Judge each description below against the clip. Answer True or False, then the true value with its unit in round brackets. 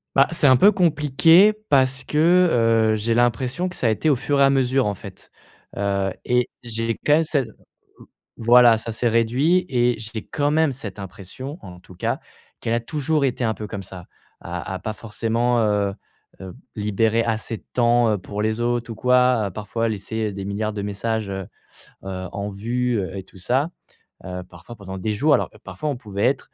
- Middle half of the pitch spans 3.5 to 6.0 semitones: True (4.2 semitones)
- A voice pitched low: True (115 Hz)